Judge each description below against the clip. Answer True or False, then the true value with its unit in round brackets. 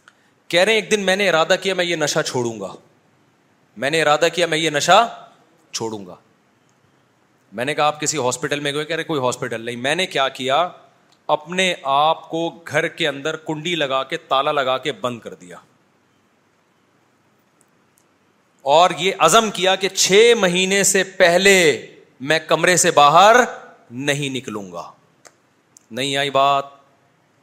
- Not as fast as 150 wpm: False (160 wpm)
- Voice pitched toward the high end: False (155 Hz)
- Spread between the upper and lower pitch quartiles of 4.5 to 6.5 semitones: True (4.8 semitones)